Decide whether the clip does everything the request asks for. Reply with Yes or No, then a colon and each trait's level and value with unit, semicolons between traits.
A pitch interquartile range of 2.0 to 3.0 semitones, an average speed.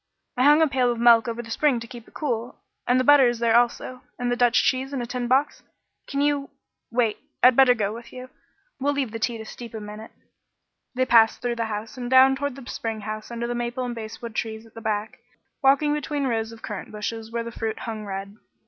No: narrow, 2.4 semitones; fast, 240 wpm